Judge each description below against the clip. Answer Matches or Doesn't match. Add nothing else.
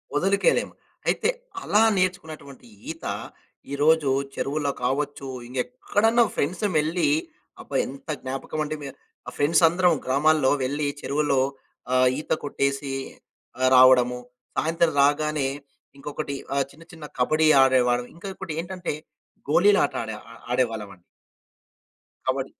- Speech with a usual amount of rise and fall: Matches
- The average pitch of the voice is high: Doesn't match